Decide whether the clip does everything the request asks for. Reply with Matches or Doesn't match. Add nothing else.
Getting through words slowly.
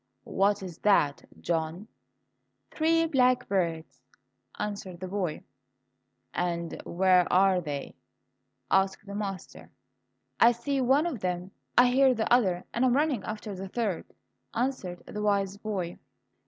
Matches